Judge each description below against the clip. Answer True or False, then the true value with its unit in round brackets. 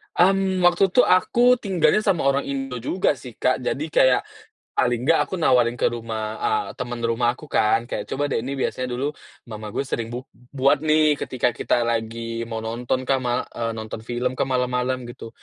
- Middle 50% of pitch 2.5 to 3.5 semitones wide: False (4.1 semitones)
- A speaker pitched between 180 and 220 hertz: False (130 Hz)